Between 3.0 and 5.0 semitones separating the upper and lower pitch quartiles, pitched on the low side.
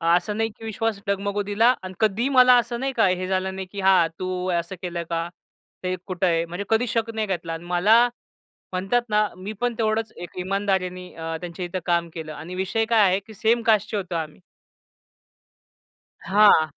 No: average, 3.7 semitones; high, 195 Hz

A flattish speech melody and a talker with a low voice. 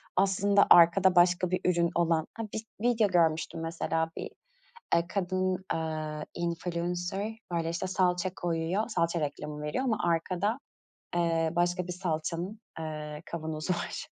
No: narrow, 2.3 semitones; medium, 175 Hz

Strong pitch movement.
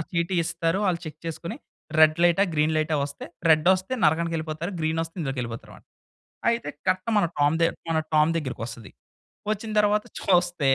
No: average, 2.7 semitones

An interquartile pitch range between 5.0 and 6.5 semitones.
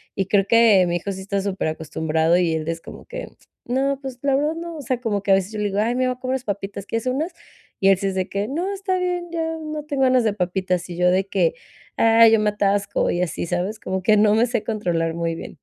Yes: wide, 5.6 semitones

